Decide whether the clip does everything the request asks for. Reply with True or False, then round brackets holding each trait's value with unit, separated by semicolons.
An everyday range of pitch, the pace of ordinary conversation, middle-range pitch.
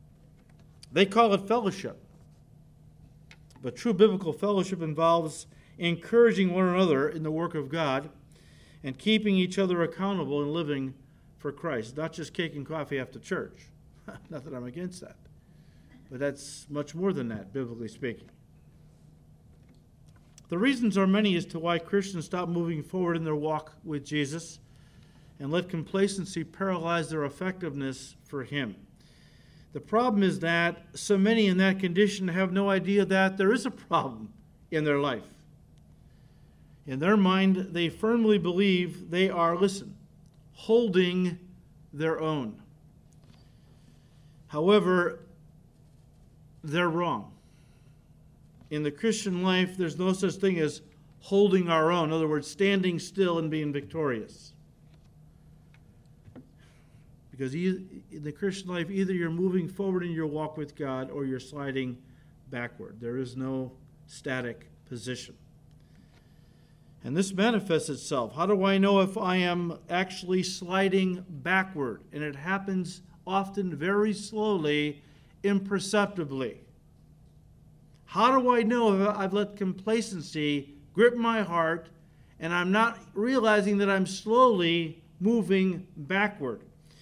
False (4.6 semitones; 130 wpm; 170 Hz)